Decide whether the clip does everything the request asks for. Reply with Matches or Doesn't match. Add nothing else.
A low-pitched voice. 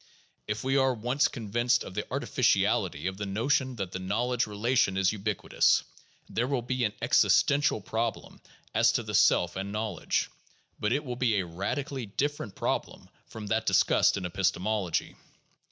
Matches